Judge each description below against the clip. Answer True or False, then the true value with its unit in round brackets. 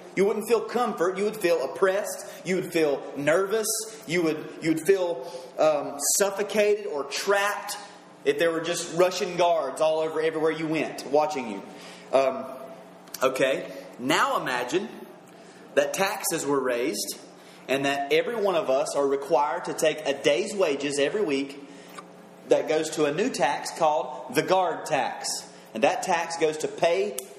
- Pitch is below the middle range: False (160 Hz)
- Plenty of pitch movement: True (5.7 semitones)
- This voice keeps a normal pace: True (160 wpm)